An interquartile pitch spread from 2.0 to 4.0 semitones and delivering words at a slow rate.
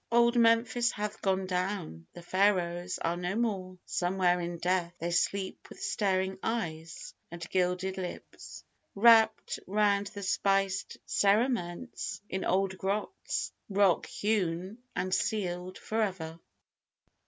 Yes: average, 2.8 semitones; slow, 120 wpm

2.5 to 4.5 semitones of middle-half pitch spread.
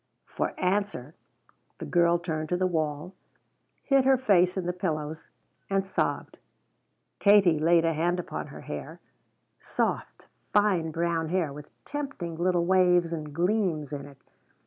Yes: average, 3.0 semitones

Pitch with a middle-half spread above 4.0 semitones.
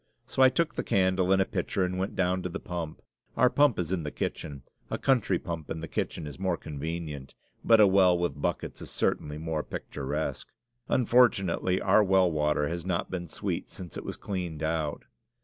No: average, 3.4 semitones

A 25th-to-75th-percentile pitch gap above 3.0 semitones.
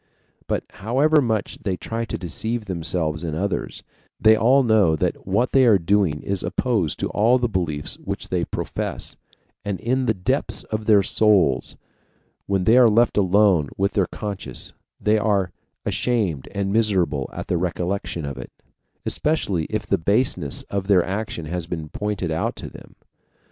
Yes: average, 4.0 semitones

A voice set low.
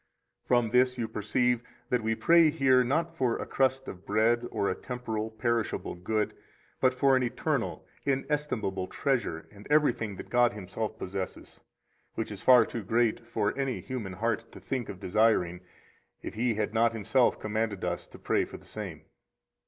Yes: low, 115 Hz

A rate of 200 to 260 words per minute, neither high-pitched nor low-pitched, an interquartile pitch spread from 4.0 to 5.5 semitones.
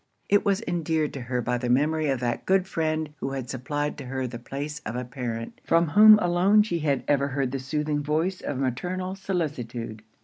Yes: fast, 205 wpm; medium, 145 Hz; average, 5.2 semitones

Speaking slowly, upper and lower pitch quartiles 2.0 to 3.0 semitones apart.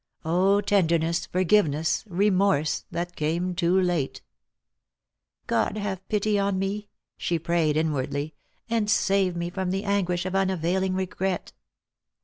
Yes: slow, 130 wpm; narrow, 2.6 semitones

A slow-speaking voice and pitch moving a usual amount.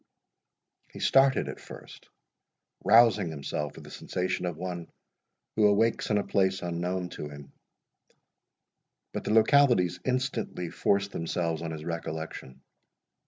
Yes: slow, 125 wpm; average, 4.5 semitones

